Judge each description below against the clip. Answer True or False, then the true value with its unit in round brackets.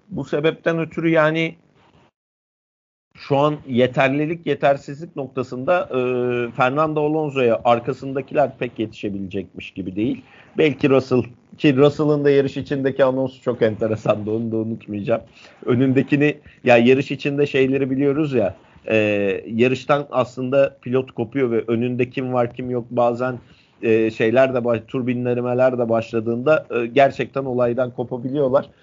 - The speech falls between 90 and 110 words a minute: False (125 wpm)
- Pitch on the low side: True (130 Hz)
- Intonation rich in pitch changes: False (3.1 semitones)